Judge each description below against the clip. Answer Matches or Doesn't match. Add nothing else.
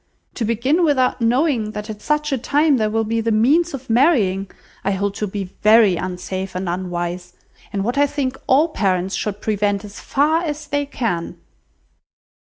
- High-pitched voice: Matches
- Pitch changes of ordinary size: Doesn't match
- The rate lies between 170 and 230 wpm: Matches